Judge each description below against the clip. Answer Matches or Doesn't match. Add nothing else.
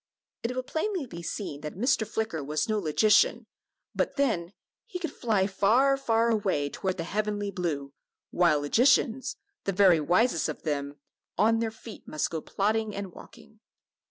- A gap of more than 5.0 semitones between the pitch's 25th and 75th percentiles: Matches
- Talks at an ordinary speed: Matches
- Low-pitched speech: Doesn't match